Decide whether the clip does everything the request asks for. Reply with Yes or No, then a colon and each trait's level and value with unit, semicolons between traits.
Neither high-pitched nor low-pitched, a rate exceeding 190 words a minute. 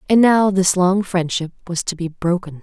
Yes: medium, 180 Hz; fast, 205 wpm